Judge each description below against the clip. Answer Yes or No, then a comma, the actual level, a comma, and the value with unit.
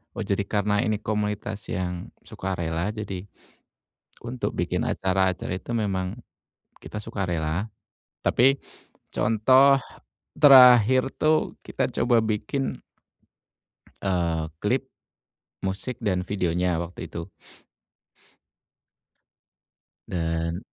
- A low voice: Yes, low, 100 Hz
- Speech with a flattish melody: No, average, 4.1 semitones